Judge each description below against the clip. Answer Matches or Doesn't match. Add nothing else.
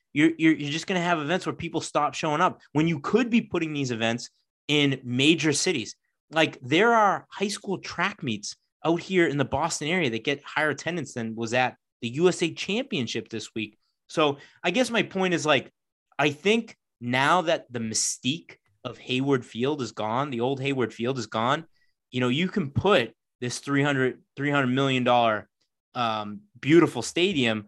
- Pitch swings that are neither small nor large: Doesn't match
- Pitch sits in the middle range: Matches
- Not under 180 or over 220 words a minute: Matches